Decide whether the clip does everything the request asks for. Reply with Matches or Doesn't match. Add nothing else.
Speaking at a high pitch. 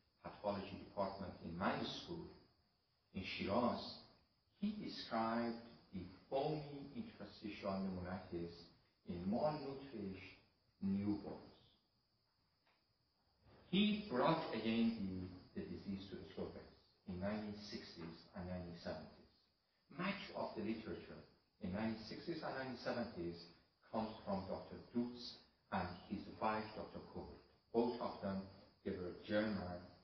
Doesn't match